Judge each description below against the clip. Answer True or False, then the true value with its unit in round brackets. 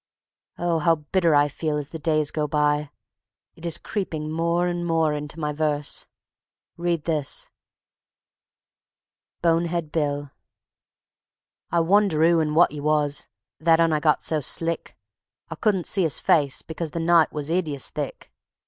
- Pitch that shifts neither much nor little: False (2.1 semitones)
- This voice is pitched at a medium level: True (160 Hz)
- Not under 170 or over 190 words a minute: False (150 wpm)